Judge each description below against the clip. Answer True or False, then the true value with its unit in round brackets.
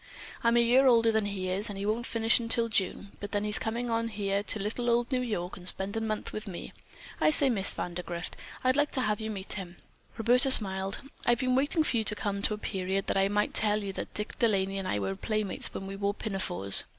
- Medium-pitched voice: False (210 Hz)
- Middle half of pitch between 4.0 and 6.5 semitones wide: False (3.2 semitones)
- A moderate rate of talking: False (245 wpm)